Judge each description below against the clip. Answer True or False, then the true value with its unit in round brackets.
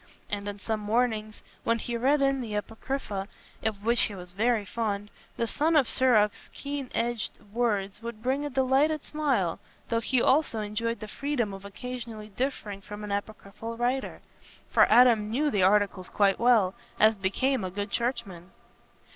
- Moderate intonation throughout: True (3.6 semitones)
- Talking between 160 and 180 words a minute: True (165 wpm)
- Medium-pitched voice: False (225 Hz)